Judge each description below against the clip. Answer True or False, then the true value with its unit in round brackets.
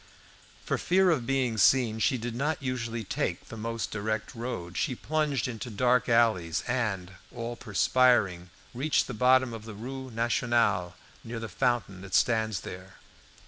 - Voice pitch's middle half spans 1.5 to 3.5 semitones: True (2.8 semitones)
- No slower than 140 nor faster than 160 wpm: True (155 wpm)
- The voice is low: True (115 Hz)